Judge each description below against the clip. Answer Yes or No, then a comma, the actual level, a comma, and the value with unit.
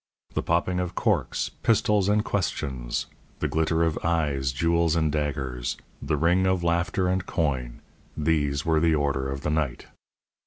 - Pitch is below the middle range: Yes, very low, 80 Hz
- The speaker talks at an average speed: Yes, average, 155 wpm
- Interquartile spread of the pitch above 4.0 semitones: No, average, 3.6 semitones